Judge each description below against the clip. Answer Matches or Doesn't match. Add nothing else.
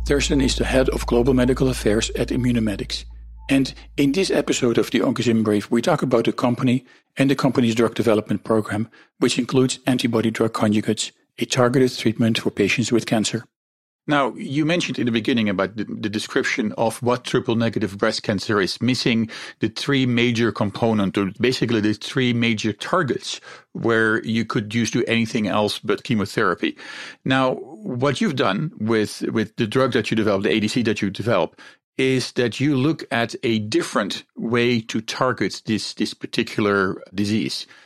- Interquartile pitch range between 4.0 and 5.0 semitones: Doesn't match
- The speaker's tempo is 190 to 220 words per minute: Doesn't match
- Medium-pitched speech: Doesn't match